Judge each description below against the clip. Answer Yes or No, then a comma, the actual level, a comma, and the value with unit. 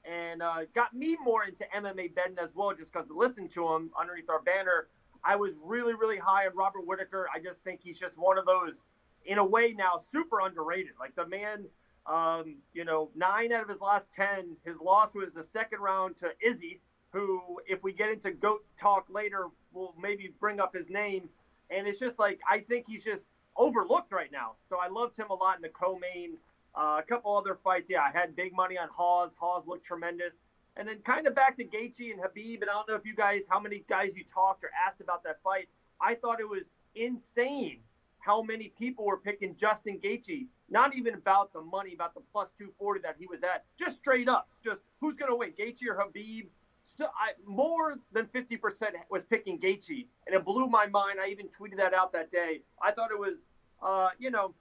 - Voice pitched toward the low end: No, high, 195 Hz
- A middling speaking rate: No, fast, 220 wpm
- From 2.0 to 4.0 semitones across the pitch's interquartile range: Yes, average, 3.6 semitones